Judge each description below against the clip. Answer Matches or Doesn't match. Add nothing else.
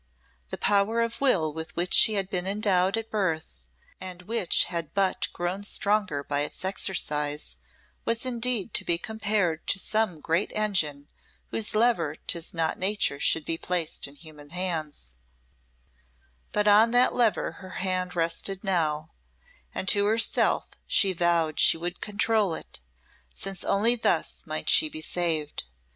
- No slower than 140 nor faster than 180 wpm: Matches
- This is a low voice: Doesn't match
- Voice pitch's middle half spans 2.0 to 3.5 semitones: Doesn't match